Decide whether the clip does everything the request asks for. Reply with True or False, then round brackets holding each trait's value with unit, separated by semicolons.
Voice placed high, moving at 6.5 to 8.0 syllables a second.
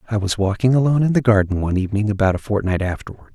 False (105 Hz; 7.7 syllables/s)